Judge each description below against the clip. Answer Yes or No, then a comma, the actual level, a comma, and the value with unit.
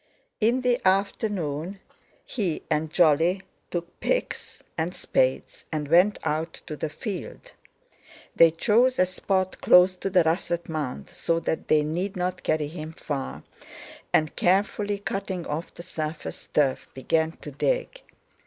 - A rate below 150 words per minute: Yes, average, 140 wpm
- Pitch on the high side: No, medium, 175 Hz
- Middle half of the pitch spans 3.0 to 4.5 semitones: Yes, average, 3.8 semitones